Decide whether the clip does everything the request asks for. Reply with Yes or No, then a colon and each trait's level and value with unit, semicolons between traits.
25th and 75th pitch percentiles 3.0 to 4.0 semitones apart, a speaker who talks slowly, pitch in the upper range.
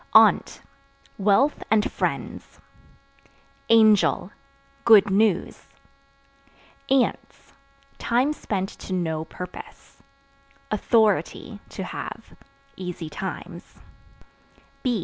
Yes: average, 3.4 semitones; slow, 70 wpm; high, 205 Hz